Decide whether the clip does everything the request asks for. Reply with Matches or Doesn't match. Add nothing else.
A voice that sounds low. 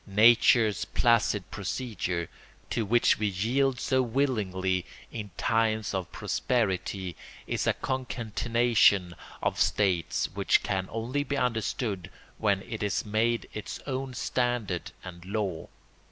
Matches